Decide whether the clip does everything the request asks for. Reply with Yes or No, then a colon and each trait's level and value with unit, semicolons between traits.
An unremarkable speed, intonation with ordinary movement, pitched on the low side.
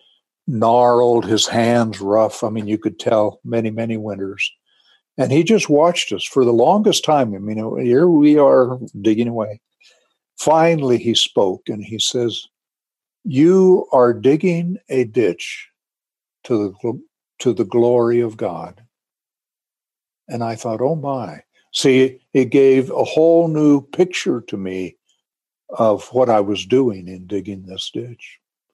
Yes: average, 145 wpm; average, 3.9 semitones; low, 120 Hz